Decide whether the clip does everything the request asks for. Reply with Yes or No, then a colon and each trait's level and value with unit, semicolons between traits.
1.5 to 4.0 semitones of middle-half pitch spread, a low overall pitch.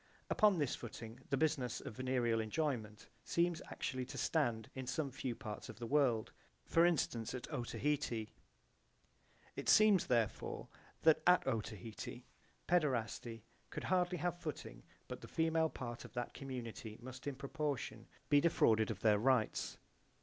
No: average, 5.1 semitones; low, 130 Hz